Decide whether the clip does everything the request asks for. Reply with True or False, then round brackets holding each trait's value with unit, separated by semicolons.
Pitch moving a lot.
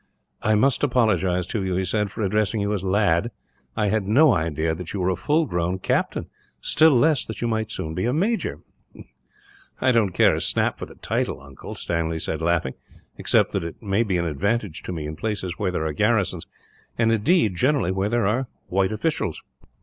False (4.8 semitones)